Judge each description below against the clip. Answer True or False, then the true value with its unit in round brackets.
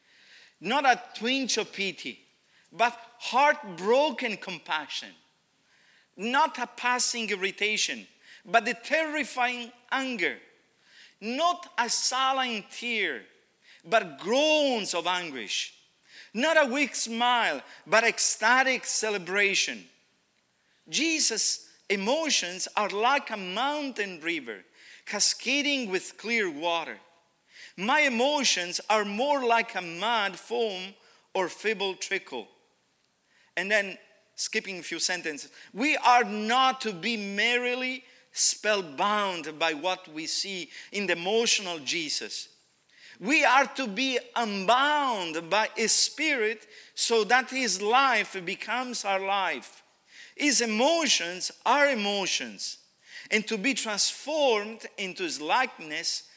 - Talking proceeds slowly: True (105 wpm)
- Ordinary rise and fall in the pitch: True (4.7 semitones)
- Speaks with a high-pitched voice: True (230 Hz)